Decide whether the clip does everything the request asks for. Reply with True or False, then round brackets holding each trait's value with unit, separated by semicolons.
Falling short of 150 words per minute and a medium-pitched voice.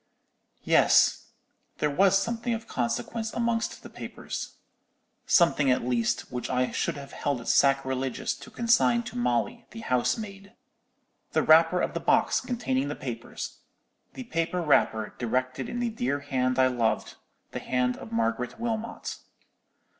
True (140 wpm; 145 Hz)